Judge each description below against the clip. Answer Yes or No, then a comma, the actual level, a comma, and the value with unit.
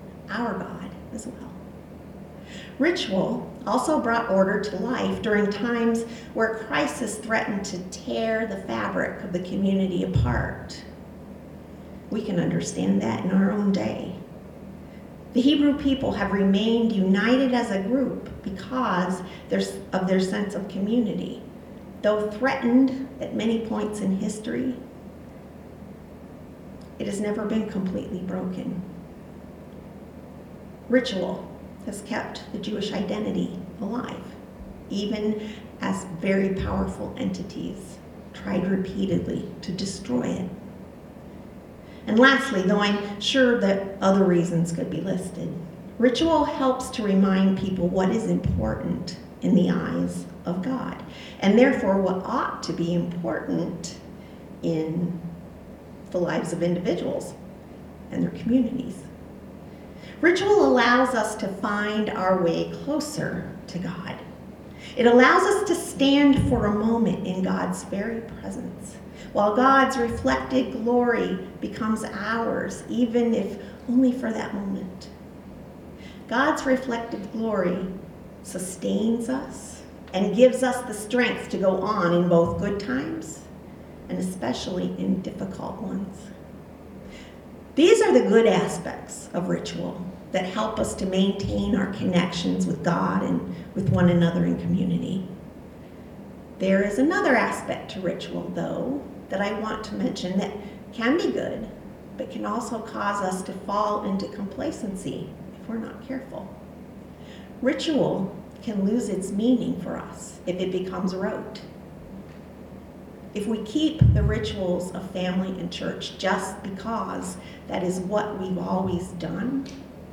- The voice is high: Yes, high, 205 Hz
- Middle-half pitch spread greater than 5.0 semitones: No, average, 4.0 semitones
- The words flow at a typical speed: No, slow, 125 wpm